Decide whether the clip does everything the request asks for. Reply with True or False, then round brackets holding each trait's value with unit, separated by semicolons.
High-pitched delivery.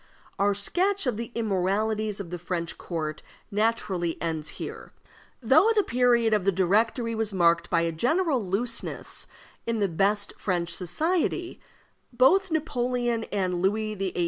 True (210 Hz)